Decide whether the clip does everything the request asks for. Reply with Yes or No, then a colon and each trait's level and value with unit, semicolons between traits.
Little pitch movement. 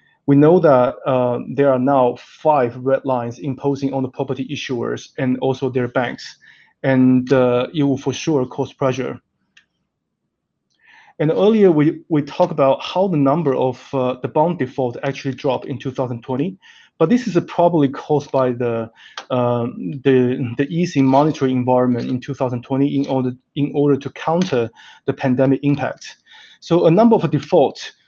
Yes: narrow, 2.3 semitones